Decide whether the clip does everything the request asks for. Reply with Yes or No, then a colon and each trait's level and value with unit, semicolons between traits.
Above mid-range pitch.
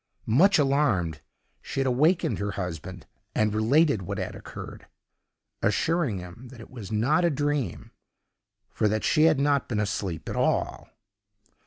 No: low, 115 Hz